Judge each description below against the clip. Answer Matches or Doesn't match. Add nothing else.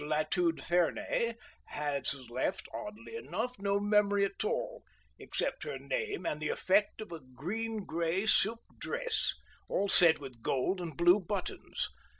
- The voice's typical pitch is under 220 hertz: Matches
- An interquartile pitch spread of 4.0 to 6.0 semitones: Matches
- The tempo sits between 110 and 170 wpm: Matches